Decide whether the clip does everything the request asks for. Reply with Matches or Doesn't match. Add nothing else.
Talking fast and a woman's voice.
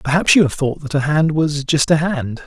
Doesn't match